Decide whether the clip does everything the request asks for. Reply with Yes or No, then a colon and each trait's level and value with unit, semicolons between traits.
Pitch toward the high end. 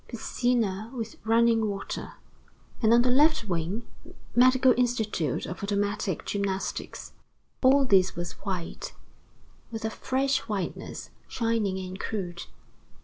Yes: high, 220 Hz